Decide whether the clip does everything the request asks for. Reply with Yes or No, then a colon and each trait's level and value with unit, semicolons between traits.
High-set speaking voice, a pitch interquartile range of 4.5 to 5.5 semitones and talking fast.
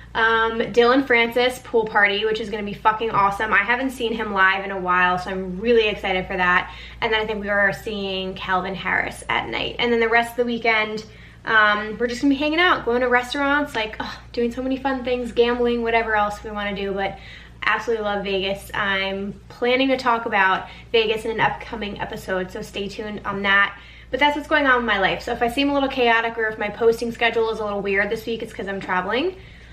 No: high, 220 Hz; average, 3.3 semitones; fast, 240 wpm